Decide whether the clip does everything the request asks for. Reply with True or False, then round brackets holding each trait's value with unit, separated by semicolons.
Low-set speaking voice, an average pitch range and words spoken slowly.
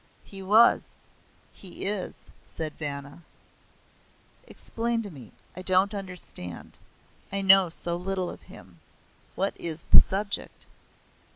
False (185 Hz; 3.5 semitones; 115 wpm)